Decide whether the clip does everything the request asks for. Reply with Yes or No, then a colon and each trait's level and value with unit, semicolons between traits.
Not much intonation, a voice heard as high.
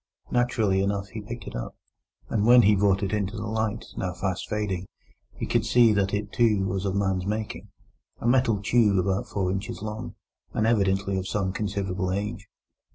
No: narrow, 2.1 semitones; low, 100 Hz